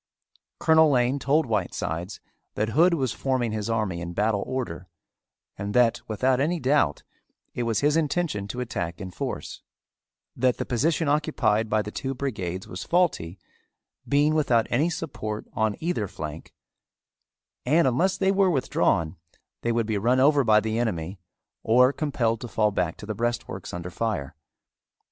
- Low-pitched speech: Yes, low, 115 Hz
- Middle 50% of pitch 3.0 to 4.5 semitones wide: No, wide, 5.5 semitones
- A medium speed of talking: Yes, average, 160 wpm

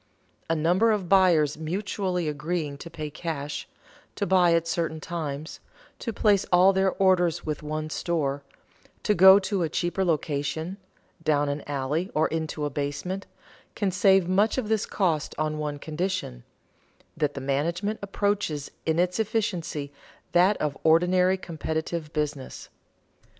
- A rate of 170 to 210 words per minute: No, average, 145 wpm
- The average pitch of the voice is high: No, medium, 170 Hz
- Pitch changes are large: No, average, 3.9 semitones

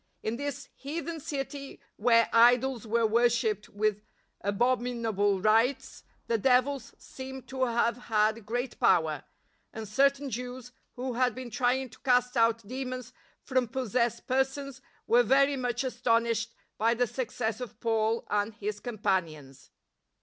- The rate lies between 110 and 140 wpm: Yes, slow, 135 wpm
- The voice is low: No, high, 240 Hz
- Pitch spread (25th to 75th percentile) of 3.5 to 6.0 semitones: No, average, 2.8 semitones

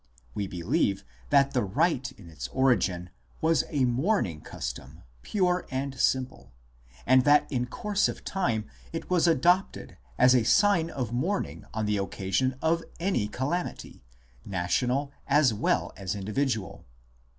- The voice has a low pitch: Yes, low, 130 Hz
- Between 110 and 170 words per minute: Yes, average, 140 wpm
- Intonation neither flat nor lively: No, wide, 7.6 semitones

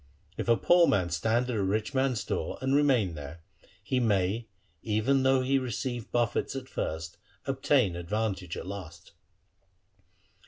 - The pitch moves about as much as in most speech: No, wide, 5.7 semitones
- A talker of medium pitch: No, low, 110 Hz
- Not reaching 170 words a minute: Yes, average, 150 wpm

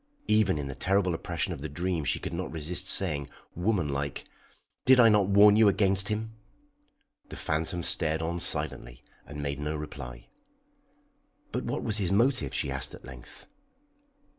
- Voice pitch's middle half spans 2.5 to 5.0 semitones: No, wide, 5.6 semitones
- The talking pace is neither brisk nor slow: Yes, average, 165 wpm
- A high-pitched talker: No, very low, 85 Hz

